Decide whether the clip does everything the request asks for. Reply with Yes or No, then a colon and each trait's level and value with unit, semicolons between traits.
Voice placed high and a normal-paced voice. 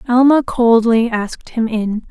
Yes: high, 235 Hz; average, 145 wpm